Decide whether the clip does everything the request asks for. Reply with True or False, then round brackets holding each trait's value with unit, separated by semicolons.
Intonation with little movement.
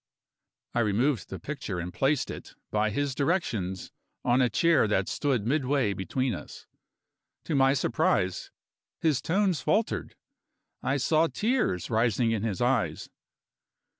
False (5.5 semitones)